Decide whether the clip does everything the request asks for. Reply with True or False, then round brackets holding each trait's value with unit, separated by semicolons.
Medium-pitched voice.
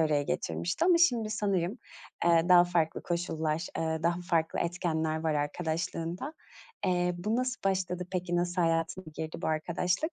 True (175 Hz)